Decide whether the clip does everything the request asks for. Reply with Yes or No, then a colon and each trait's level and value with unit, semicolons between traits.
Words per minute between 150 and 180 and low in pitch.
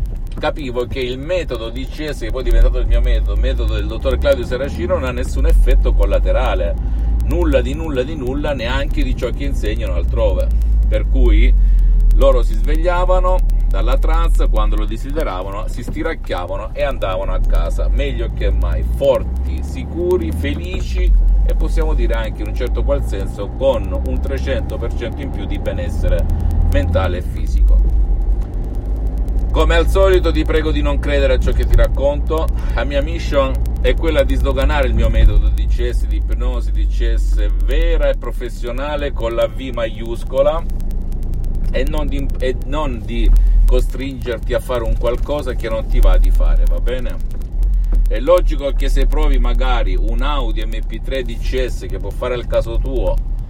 Yes: average, 165 wpm; low, 110 Hz